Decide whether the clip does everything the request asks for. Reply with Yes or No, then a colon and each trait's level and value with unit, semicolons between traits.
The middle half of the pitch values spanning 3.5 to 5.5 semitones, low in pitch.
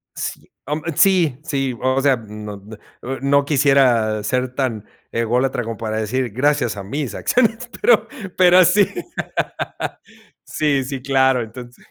Yes: average, 3.9 semitones; low, 130 Hz